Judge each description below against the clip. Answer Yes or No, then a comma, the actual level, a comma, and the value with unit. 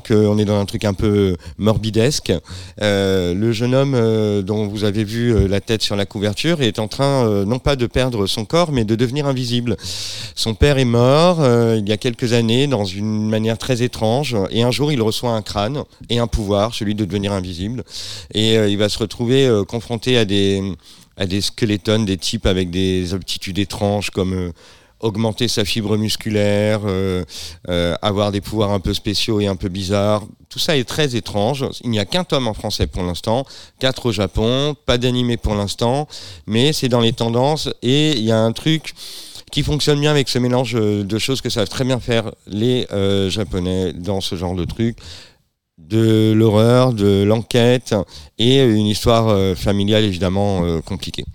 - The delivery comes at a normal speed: Yes, average, 195 wpm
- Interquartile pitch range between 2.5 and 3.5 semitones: Yes, average, 3.2 semitones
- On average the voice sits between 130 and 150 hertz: No, low, 110 Hz